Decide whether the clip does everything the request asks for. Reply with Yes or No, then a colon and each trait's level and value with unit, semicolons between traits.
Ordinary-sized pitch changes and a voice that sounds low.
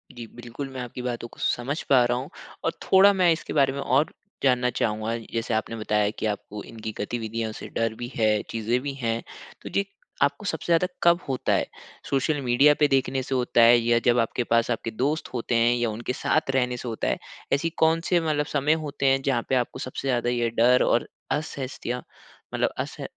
Yes: average, 3.2 semitones; low, 125 Hz